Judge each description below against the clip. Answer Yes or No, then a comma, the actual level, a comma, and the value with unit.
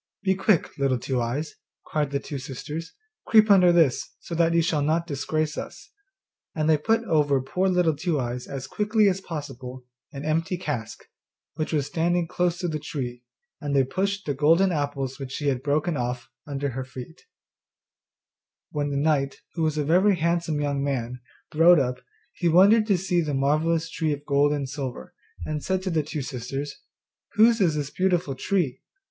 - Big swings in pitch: No, average, 4.0 semitones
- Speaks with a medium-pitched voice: Yes, medium, 150 Hz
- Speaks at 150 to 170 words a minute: No, average, 185 wpm